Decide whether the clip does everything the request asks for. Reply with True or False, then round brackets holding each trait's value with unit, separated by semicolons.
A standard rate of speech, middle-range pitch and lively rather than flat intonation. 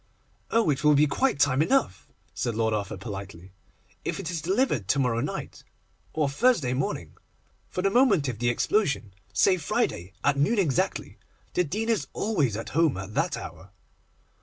True (170 wpm; 145 Hz; 8.5 semitones)